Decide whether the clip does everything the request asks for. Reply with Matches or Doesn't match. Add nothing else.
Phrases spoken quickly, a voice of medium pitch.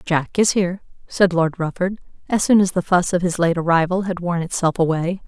Matches